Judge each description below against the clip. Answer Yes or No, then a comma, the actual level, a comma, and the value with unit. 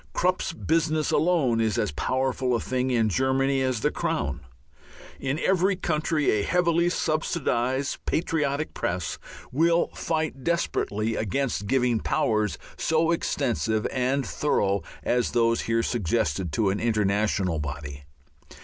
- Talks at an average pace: No, slow, 125 wpm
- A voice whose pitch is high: No, low, 130 Hz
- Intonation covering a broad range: Yes, wide, 6.4 semitones